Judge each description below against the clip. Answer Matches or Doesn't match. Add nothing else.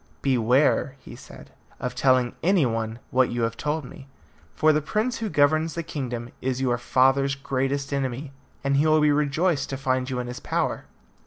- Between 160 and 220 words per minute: Matches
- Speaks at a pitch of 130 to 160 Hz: Matches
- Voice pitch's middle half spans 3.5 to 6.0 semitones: Doesn't match